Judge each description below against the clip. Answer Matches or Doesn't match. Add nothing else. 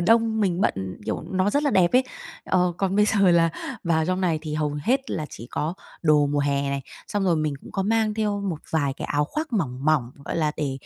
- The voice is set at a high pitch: Doesn't match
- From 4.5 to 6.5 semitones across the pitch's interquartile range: Matches